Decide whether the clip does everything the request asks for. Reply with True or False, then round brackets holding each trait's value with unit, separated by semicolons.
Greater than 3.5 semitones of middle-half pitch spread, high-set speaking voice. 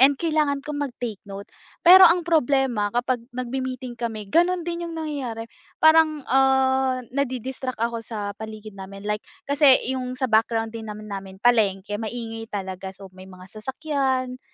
True (4.4 semitones; 250 Hz)